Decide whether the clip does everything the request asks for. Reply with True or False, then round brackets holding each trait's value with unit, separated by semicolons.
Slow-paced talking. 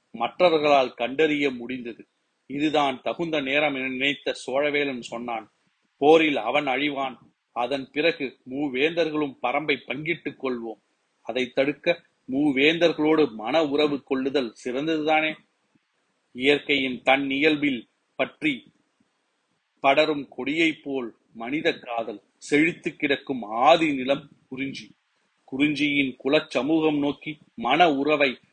False (95 wpm)